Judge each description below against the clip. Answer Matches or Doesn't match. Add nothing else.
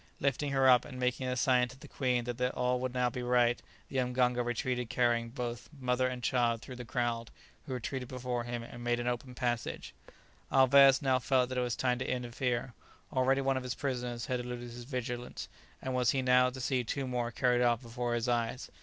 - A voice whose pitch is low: Matches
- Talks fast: Matches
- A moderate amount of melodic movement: Doesn't match